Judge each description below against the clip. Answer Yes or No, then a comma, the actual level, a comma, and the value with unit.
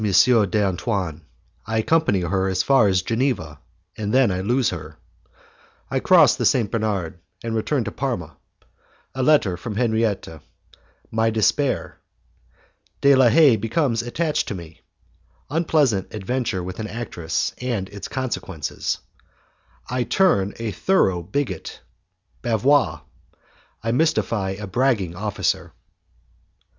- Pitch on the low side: Yes, low, 110 Hz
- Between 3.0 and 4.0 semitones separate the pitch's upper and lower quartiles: No, average, 5.2 semitones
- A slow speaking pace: Yes, slow, 120 wpm